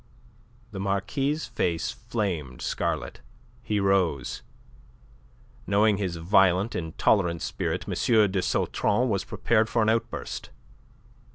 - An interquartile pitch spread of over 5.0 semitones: No, average, 3.6 semitones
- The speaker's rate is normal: No, slow, 105 wpm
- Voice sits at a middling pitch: No, low, 100 Hz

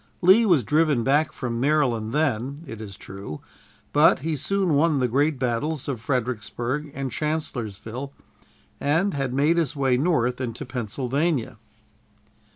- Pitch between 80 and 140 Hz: Yes, low, 135 Hz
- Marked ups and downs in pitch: No, average, 4.3 semitones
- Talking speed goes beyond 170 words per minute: No, average, 140 wpm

